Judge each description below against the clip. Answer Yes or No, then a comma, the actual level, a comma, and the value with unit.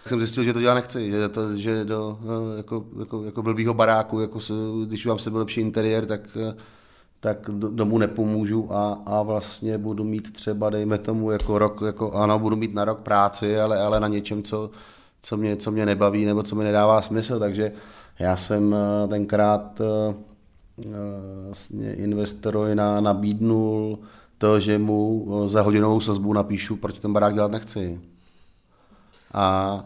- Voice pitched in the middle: No, low, 105 Hz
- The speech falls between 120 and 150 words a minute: No, average, 160 wpm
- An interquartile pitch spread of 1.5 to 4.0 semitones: No, narrow, 1.0 semitones